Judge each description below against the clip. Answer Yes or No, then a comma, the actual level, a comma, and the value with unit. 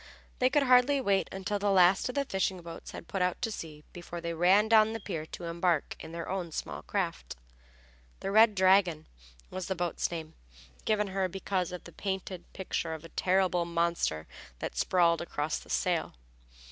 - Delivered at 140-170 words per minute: No, average, 185 wpm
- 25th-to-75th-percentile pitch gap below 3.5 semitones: Yes, average, 2.9 semitones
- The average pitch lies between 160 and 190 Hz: Yes, medium, 185 Hz